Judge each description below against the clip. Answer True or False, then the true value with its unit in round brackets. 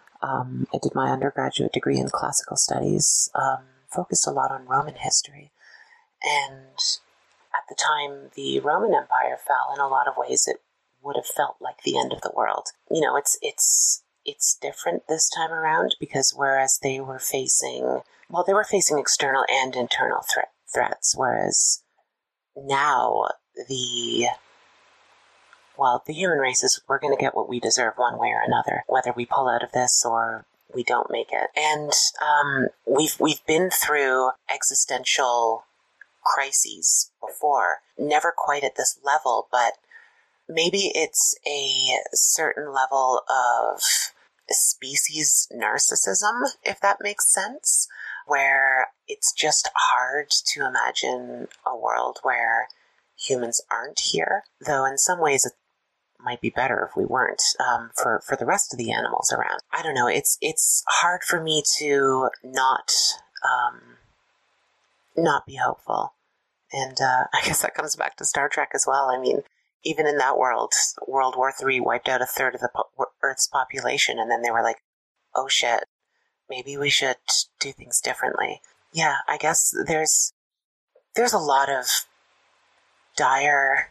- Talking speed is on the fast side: False (155 wpm)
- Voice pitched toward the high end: False (150 Hz)